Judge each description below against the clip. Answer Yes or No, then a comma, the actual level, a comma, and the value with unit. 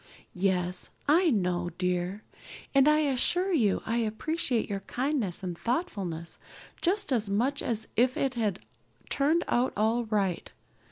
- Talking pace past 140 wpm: No, slow, 135 wpm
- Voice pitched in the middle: No, high, 230 Hz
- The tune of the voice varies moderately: No, wide, 6.5 semitones